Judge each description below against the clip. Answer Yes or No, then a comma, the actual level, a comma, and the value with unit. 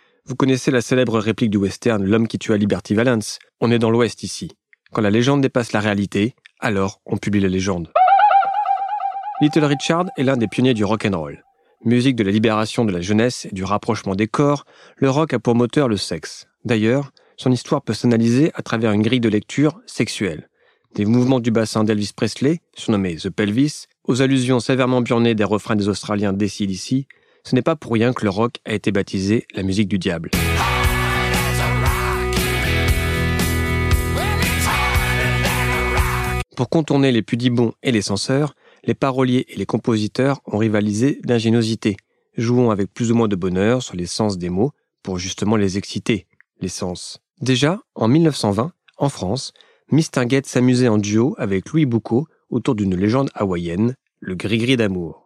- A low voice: Yes, low, 115 Hz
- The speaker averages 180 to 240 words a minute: No, average, 165 wpm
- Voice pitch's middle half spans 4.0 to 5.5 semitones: Yes, average, 4.5 semitones